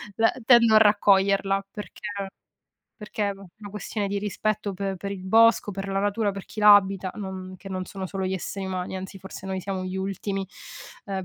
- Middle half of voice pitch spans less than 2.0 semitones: Yes, narrow, 1.4 semitones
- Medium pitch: No, high, 195 Hz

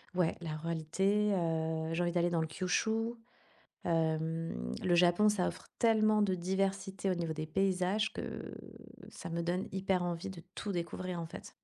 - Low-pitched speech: No, medium, 175 Hz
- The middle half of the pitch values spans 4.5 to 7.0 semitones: No, average, 2.8 semitones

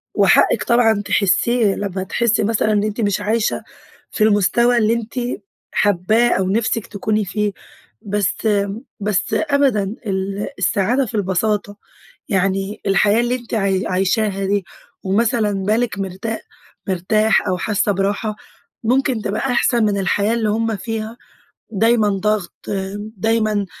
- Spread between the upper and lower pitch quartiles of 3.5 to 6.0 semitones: No, narrow, 2.4 semitones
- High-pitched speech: Yes, high, 210 Hz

